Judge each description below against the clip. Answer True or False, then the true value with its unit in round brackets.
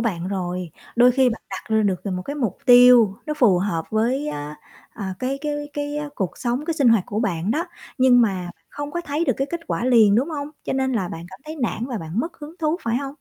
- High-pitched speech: True (240 Hz)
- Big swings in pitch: True (6.6 semitones)